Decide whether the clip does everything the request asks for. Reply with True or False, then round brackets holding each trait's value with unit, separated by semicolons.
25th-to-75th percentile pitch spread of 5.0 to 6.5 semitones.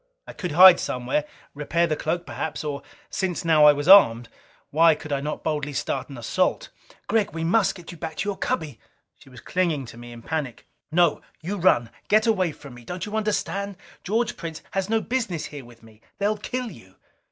True (5.4 semitones)